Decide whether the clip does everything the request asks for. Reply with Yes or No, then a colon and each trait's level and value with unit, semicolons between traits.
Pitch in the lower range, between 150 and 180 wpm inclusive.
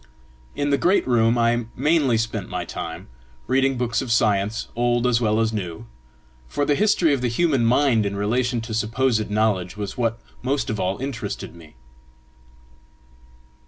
Yes: low, 115 Hz; average, 160 wpm